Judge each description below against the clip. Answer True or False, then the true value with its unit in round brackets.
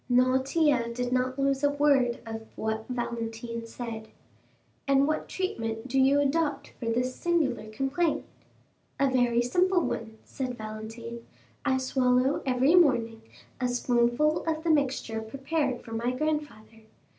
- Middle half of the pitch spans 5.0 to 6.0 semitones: False (3.5 semitones)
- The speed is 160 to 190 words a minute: False (135 wpm)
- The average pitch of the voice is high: True (255 Hz)